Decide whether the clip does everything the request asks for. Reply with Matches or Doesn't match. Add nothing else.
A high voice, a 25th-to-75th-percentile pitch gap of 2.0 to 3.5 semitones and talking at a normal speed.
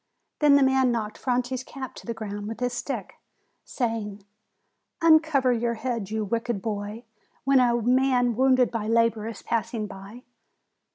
Matches